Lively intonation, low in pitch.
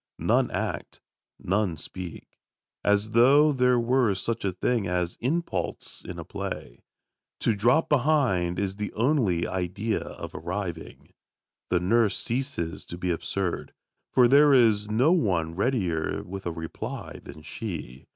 Yes: wide, 5.8 semitones; low, 105 Hz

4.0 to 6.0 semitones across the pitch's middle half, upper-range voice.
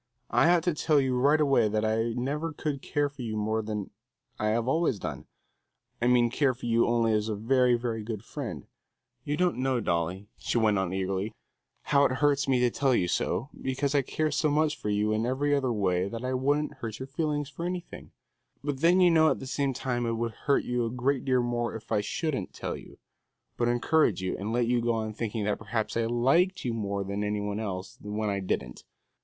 No: average, 4.6 semitones; low, 120 Hz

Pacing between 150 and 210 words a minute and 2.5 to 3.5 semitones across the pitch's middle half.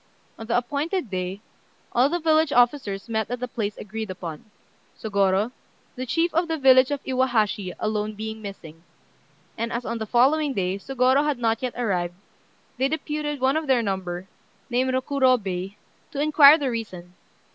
No: average, 165 wpm; wide, 5.4 semitones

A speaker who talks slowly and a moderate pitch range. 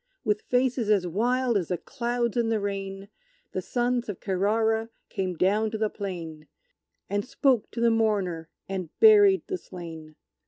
No: average, 160 wpm; average, 4.0 semitones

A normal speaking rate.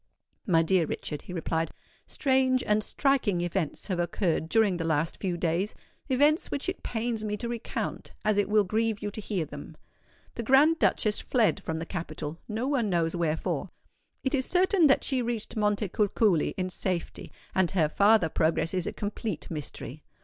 Yes: average, 170 wpm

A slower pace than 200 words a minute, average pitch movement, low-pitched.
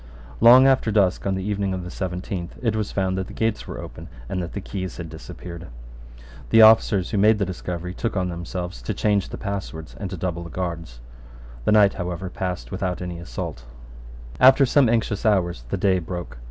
No: fast, 205 wpm; average, 3.0 semitones; very low, 95 Hz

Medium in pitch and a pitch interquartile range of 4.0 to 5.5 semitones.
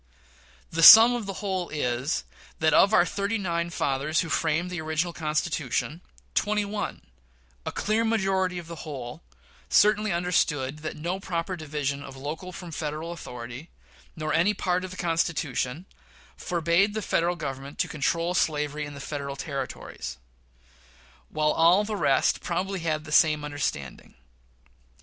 No: medium, 165 Hz; average, 3.6 semitones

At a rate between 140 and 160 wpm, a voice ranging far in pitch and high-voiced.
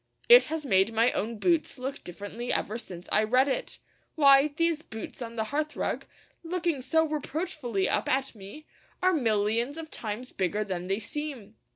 No: average, 170 wpm; wide, 6.2 semitones; very high, 255 Hz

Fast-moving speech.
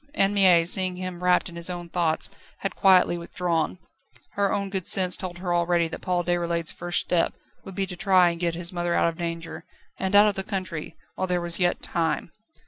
Yes: fast, 215 wpm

